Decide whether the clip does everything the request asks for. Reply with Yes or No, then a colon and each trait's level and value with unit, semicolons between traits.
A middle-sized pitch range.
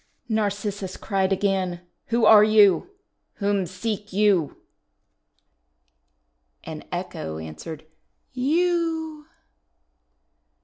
Yes: average, 3.6 semitones